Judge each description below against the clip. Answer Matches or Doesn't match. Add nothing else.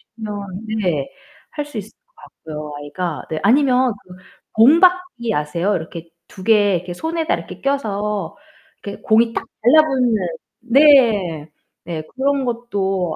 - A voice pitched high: Matches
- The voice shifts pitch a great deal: Matches